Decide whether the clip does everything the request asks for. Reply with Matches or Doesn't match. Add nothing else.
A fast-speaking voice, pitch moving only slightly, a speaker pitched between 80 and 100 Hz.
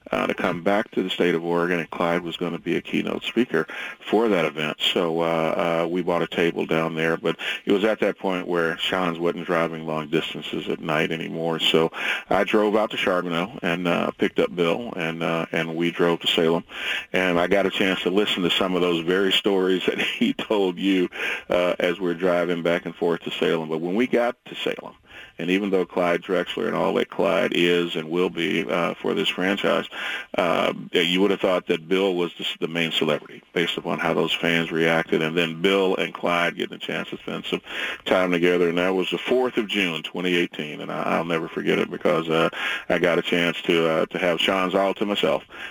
Matches